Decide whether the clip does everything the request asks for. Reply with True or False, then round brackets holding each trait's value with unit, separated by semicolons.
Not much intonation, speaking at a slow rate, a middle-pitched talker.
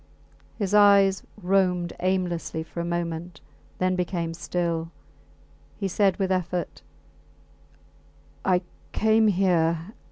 True (2.2 semitones; 105 wpm; 180 Hz)